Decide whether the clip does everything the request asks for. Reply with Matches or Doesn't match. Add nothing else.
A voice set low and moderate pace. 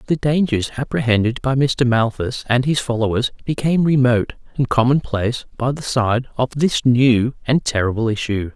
Matches